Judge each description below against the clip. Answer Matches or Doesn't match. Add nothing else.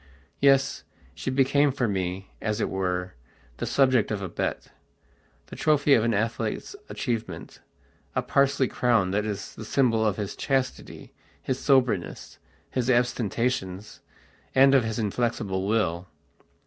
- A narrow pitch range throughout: Doesn't match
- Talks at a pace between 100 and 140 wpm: Matches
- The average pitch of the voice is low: Matches